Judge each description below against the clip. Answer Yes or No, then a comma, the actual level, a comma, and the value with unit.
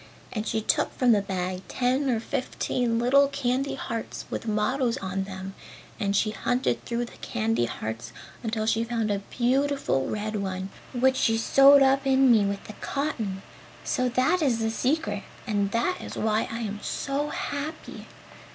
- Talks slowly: No, average, 170 wpm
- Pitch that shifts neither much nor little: Yes, average, 4.5 semitones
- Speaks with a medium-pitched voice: No, high, 230 Hz